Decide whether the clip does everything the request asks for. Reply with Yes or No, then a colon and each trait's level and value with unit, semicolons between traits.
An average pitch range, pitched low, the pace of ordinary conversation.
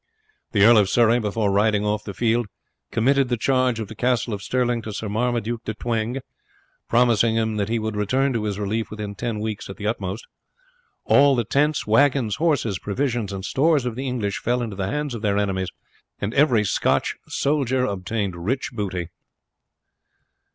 Yes: average, 3.2 semitones; low, 115 Hz; average, 180 wpm